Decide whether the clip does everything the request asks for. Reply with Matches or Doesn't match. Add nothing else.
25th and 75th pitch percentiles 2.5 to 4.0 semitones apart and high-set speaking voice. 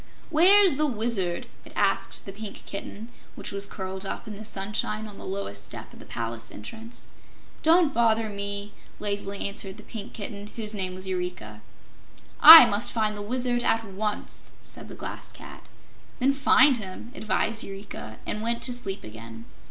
Matches